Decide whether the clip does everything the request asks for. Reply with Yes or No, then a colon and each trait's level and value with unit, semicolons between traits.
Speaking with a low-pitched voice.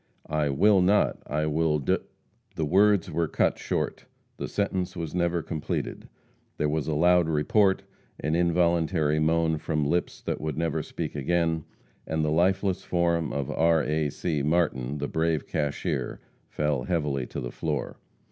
Yes: very low, 80 Hz